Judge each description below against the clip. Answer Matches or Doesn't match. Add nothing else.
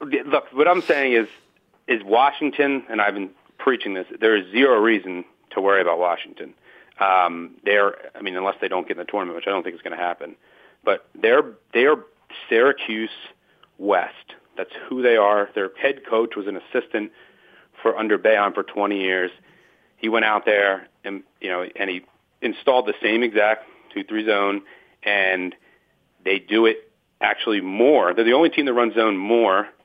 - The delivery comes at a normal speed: Matches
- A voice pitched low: Matches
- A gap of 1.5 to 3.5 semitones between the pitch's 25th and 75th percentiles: Matches